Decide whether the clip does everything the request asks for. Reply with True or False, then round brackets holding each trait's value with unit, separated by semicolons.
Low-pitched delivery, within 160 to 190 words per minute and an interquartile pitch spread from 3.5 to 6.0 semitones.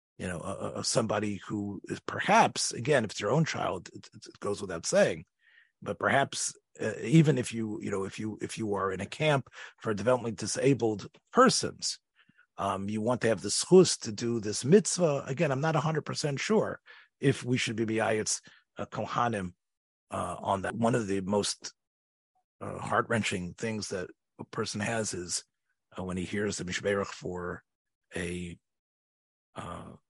True (110 Hz; 170 wpm; 4.0 semitones)